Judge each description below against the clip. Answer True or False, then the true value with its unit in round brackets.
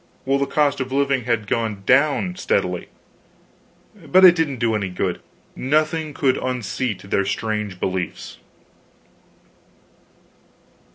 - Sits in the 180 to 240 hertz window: False (130 Hz)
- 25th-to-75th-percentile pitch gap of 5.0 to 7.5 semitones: True (5.3 semitones)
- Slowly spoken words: True (115 wpm)